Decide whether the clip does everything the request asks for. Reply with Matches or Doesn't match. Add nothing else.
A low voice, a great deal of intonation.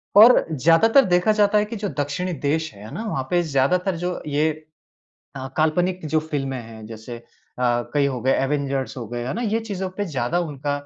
Doesn't match